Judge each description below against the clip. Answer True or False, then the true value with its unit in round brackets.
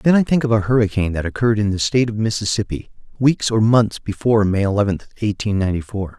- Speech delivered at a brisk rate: True (215 wpm)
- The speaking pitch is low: True (105 Hz)